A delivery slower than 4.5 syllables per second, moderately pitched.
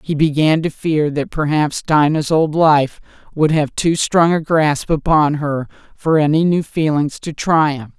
Yes: 4.1 syllables/s; medium, 155 Hz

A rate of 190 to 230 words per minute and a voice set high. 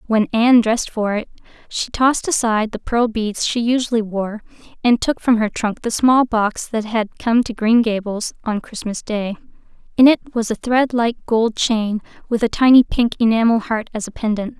Yes: average, 195 wpm; high, 225 Hz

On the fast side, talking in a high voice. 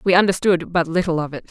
No: fast, 240 wpm; medium, 170 Hz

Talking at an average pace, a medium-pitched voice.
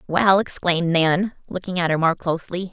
Yes: average, 175 wpm; medium, 175 Hz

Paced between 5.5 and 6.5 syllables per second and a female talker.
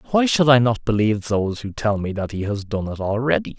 No: 6.0 syllables/s; male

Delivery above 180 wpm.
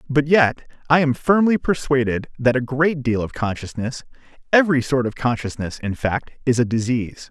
No: average, 175 wpm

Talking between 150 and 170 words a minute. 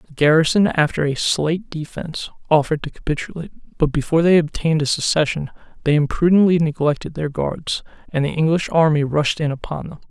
Yes: average, 165 wpm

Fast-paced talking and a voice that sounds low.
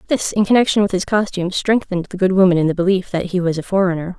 No: fast, 260 wpm; medium, 185 Hz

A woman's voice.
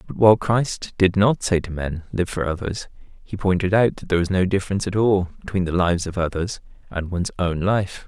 No: male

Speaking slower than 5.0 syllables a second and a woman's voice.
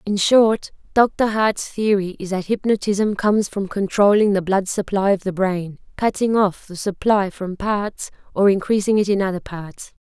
Yes: 4.5 syllables/s; female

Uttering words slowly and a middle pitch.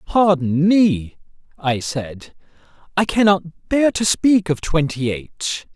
Yes: slow, 125 wpm; medium, 165 Hz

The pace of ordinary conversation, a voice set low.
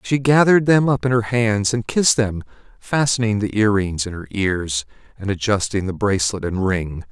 Yes: average, 195 wpm; low, 105 Hz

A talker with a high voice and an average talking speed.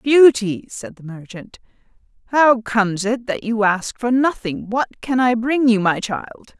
Yes: high, 230 Hz; average, 175 wpm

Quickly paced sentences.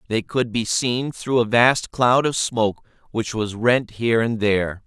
No: average, 195 wpm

